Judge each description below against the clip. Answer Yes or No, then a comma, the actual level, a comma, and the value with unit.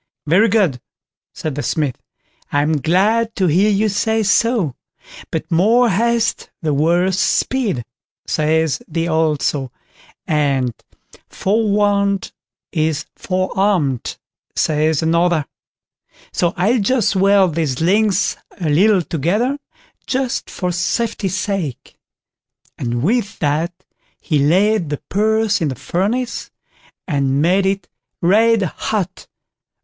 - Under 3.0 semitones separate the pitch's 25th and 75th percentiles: No, average, 5.1 semitones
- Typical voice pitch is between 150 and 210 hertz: Yes, medium, 185 Hz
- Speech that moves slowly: Yes, slow, 115 wpm